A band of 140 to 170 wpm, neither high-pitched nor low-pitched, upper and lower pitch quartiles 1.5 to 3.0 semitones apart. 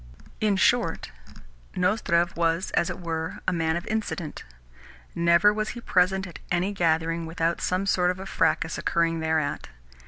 Yes: average, 155 wpm; medium, 170 Hz; narrow, 2.6 semitones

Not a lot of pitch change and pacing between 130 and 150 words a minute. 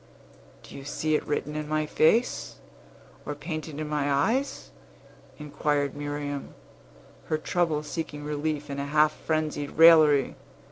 Yes: narrow, 1.3 semitones; slow, 135 wpm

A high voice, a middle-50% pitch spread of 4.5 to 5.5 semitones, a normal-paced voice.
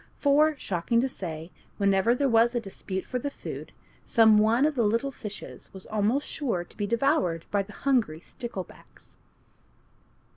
Yes: high, 225 Hz; average, 5.1 semitones; average, 160 wpm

